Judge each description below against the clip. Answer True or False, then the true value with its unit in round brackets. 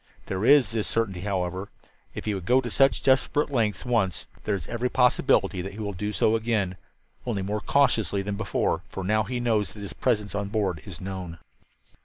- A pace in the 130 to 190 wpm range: False (200 wpm)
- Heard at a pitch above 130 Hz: False (105 Hz)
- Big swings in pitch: False (3.4 semitones)